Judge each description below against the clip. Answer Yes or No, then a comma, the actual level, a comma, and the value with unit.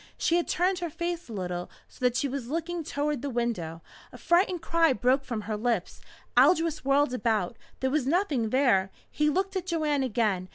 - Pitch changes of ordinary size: No, wide, 6.3 semitones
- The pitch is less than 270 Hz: No, very high, 275 Hz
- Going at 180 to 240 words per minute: Yes, average, 195 wpm